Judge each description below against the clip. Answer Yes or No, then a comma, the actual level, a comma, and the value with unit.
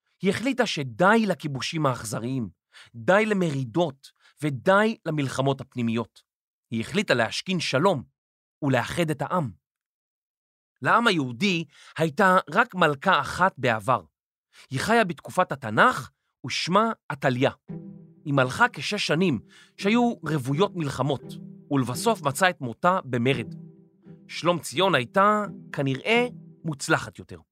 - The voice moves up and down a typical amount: No, wide, 6.0 semitones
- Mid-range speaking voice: Yes, medium, 165 Hz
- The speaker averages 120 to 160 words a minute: No, average, 105 wpm